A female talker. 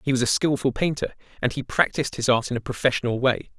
No: male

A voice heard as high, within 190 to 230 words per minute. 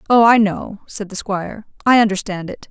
Yes: high, 210 Hz; average, 200 wpm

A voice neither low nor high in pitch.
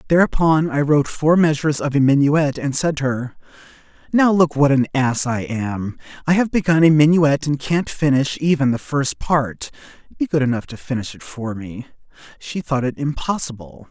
Yes: medium, 145 Hz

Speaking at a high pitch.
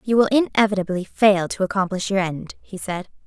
Yes: high, 195 Hz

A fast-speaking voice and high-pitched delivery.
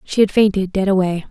Yes: fast, 230 wpm; high, 195 Hz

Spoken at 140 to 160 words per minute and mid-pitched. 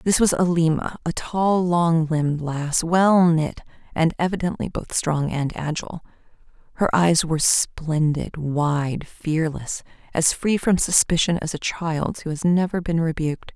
Yes: average, 150 wpm; medium, 165 Hz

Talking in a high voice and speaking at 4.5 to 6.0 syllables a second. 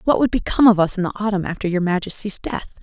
No: high, 200 Hz; 6.9 syllables/s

